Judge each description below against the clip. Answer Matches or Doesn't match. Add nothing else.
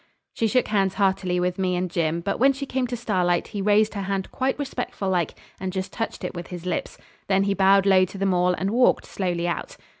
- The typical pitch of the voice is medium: Doesn't match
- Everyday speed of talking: Doesn't match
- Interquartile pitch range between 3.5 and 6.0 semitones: Doesn't match